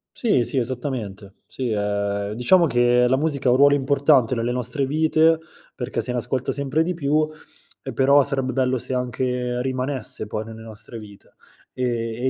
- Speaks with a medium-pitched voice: No, low, 125 Hz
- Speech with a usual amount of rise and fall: Yes, average, 3.2 semitones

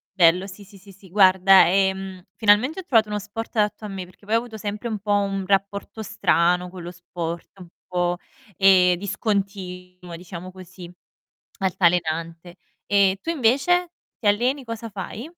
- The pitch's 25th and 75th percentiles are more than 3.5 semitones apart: No, average, 2.7 semitones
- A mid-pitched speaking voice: No, high, 195 Hz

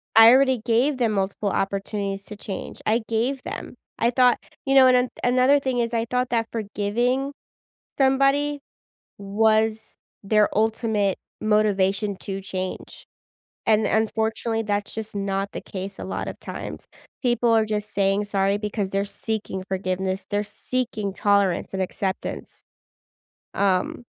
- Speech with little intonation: No, average, 3.2 semitones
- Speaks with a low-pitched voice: No, high, 215 Hz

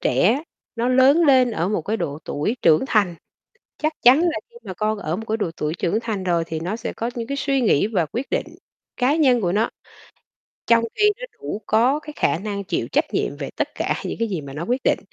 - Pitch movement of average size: No, wide, 6.5 semitones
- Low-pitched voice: No, high, 220 Hz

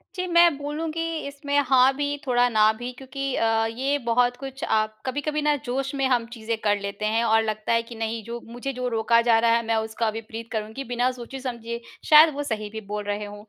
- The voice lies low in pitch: No, high, 235 Hz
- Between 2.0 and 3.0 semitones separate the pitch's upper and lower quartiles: No, average, 3.6 semitones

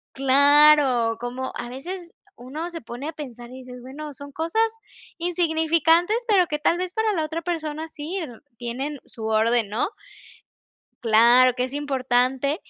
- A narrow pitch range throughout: No, average, 4.6 semitones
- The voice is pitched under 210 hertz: No, very high, 285 Hz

